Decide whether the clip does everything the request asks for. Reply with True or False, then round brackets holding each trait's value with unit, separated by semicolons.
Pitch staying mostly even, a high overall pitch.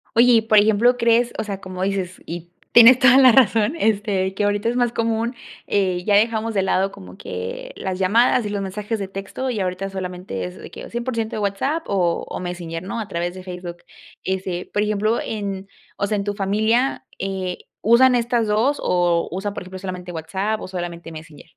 False (3.6 semitones; 200 Hz)